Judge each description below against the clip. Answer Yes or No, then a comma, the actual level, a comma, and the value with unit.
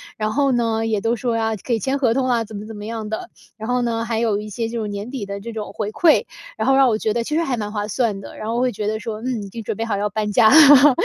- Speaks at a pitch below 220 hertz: No, high, 225 Hz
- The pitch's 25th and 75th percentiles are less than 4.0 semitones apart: Yes, narrow, 2.4 semitones